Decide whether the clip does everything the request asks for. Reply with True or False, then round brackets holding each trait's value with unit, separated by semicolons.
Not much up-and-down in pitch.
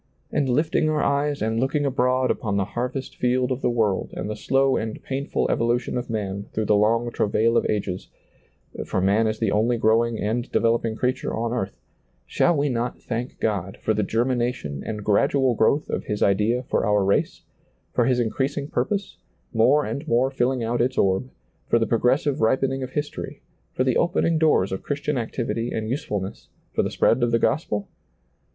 False (3.3 semitones)